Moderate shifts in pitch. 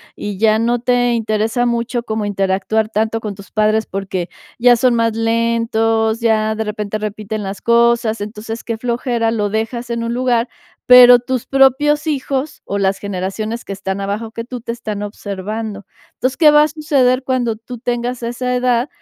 No: narrow, 2.3 semitones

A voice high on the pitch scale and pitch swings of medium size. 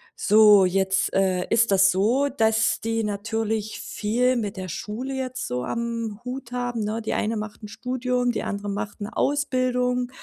Yes: high, 225 Hz; average, 3.3 semitones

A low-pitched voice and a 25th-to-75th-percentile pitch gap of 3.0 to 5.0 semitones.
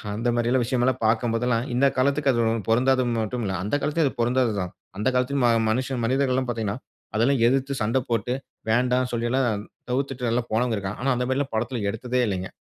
No: low, 125 Hz; narrow, 2.4 semitones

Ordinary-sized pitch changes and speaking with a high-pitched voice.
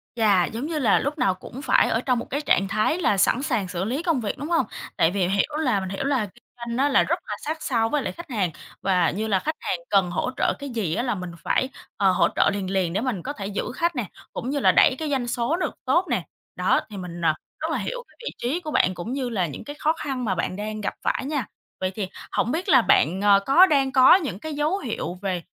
No: wide, 6.8 semitones; high, 235 Hz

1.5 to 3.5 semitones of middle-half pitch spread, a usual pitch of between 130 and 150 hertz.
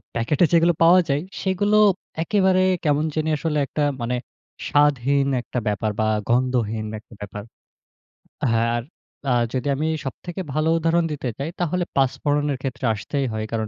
No: wide, 5.4 semitones; medium, 140 Hz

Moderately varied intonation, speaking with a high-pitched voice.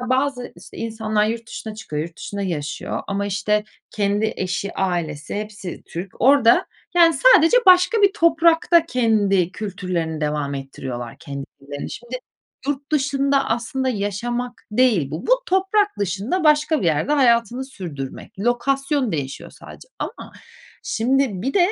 No: wide, 7.0 semitones; high, 225 Hz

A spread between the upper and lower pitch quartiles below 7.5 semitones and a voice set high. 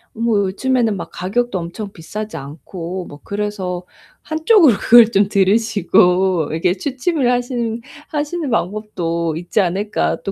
Yes: average, 5.1 semitones; high, 205 Hz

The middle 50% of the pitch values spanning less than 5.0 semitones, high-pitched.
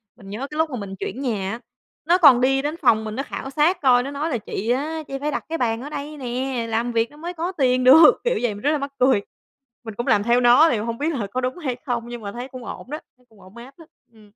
Yes: average, 4.1 semitones; very high, 255 Hz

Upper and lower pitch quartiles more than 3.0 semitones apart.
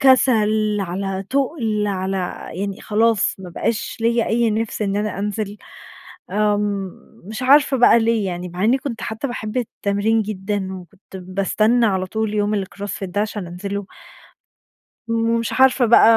No: average, 2.7 semitones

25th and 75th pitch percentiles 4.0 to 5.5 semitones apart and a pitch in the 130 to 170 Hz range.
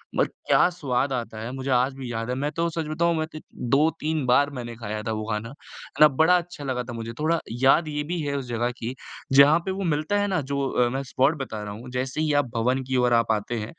Yes: average, 4.3 semitones; low, 135 Hz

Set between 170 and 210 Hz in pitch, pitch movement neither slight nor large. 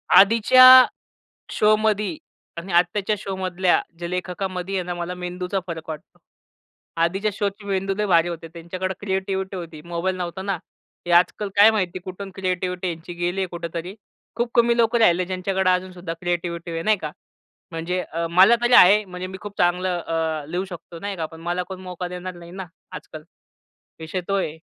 No: medium, 185 Hz; narrow, 2.0 semitones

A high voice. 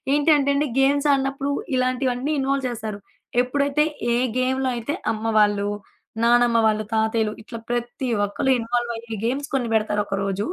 Yes: high, 240 Hz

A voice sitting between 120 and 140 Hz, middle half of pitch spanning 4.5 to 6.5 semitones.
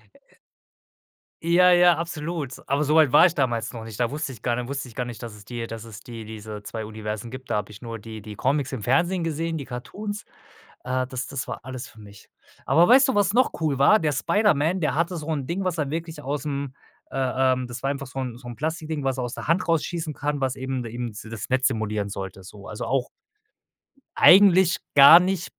Yes: low, 135 Hz; wide, 5.5 semitones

